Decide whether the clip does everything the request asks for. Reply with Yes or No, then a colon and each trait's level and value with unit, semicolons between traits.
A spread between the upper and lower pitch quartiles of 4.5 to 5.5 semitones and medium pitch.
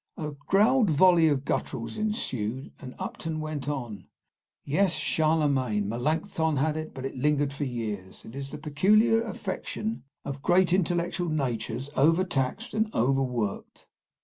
Yes: average, 5.1 semitones; medium, 150 Hz